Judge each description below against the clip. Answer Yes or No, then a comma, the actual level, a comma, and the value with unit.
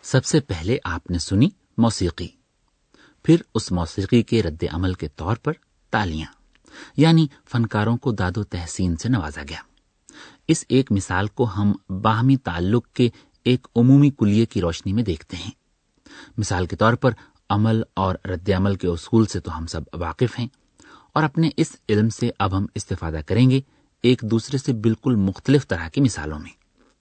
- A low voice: Yes, low, 110 Hz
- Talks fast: No, average, 170 wpm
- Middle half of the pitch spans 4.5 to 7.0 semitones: Yes, wide, 5.4 semitones